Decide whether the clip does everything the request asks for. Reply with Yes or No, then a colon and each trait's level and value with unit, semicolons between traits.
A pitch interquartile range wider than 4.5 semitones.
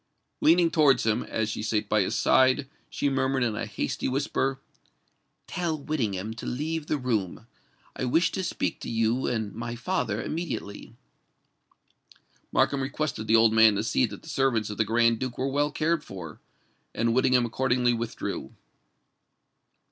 No: average, 4.1 semitones